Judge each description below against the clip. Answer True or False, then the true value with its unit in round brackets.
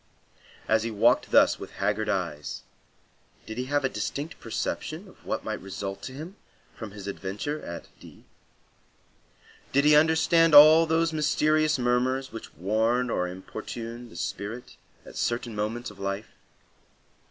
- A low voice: True (120 Hz)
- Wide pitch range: True (6.2 semitones)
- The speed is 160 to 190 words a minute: False (145 wpm)